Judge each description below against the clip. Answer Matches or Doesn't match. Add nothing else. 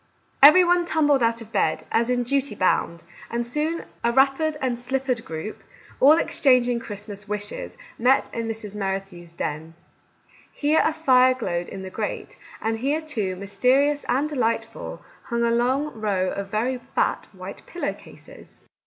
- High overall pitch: Matches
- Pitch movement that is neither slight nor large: Matches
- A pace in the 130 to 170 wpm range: Matches